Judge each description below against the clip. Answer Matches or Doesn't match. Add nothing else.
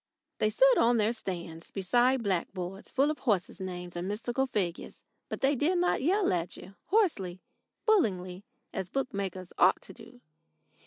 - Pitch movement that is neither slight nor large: Doesn't match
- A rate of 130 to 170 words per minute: Matches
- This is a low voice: Doesn't match